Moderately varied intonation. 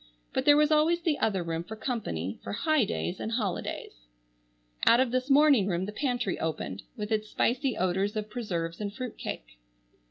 No: wide, 5.9 semitones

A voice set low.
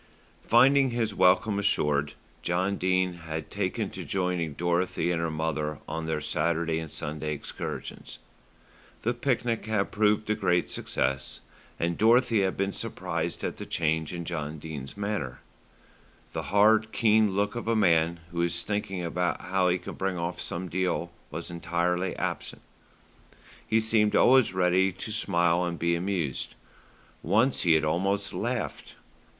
Yes: very low, 90 Hz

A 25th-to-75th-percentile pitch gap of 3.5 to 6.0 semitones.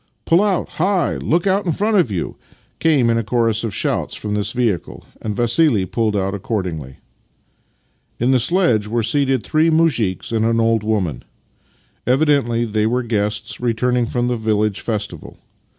Yes: average, 4.5 semitones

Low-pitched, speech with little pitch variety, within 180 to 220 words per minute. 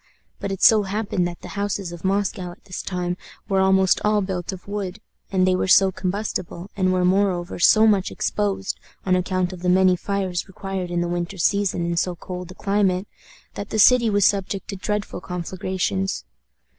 No: high, 190 Hz; narrow, 1.9 semitones; average, 190 wpm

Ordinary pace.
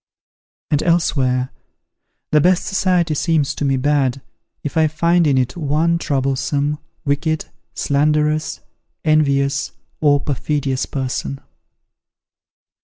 No: slow, 105 wpm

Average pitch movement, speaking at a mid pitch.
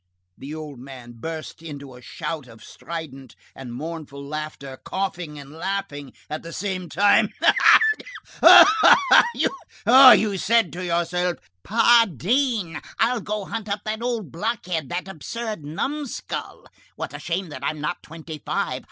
No: wide, 5.7 semitones; medium, 170 Hz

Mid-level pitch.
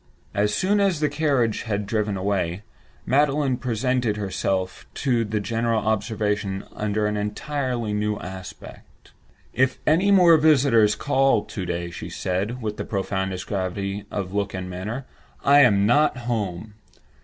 No: low, 105 Hz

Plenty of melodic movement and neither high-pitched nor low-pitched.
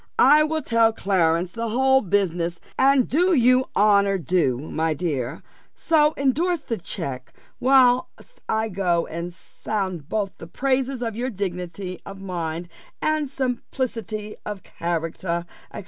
No: wide, 7.0 semitones; high, 205 Hz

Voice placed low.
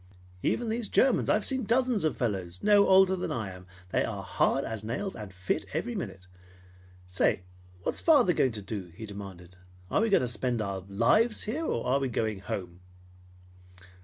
Yes: low, 120 Hz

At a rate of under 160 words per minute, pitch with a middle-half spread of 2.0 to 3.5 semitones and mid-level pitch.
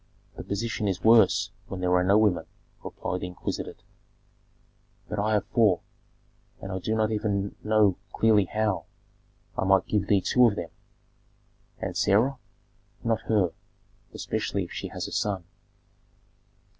No: average, 145 wpm; narrow, 2.4 semitones; low, 100 Hz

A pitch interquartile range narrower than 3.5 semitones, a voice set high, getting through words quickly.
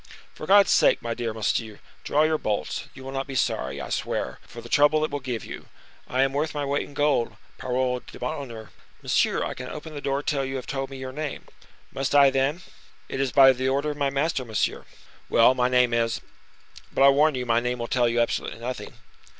No: average, 2.9 semitones; low, 135 Hz; fast, 220 wpm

